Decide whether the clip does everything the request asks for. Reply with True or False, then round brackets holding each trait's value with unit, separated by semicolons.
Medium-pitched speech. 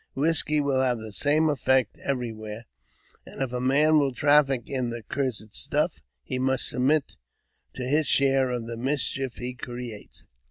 False (130 Hz)